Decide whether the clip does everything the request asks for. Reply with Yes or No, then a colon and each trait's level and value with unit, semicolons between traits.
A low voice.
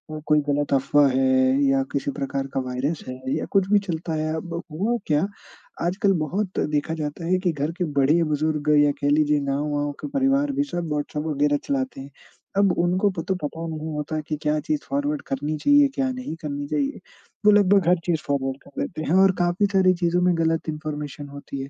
No: medium, 155 Hz